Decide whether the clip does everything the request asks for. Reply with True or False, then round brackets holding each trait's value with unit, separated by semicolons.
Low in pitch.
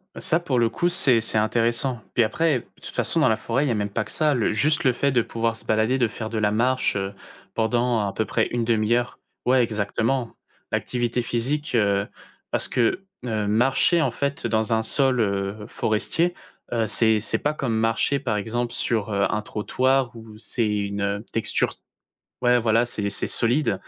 True (115 Hz)